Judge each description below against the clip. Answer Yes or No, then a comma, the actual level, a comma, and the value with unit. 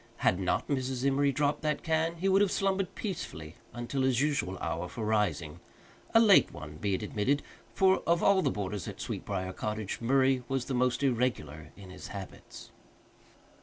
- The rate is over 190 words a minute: No, average, 175 wpm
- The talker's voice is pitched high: No, low, 125 Hz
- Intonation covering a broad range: Yes, wide, 7.6 semitones